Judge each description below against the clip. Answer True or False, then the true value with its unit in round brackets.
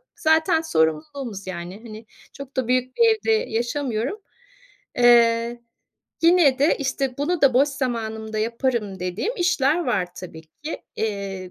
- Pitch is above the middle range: True (240 Hz)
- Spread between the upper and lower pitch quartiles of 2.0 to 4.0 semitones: False (5.1 semitones)